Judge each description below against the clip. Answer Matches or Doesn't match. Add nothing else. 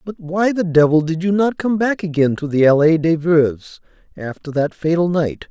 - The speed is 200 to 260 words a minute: Matches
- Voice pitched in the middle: Matches